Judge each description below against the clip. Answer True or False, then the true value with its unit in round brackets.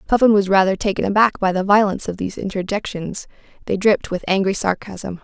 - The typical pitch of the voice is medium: False (195 Hz)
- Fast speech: False (185 wpm)